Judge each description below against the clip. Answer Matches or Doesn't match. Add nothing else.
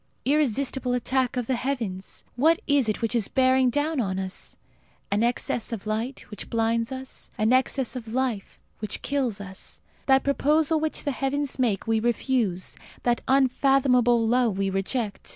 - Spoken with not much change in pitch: Doesn't match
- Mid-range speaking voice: Doesn't match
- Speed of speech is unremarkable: Matches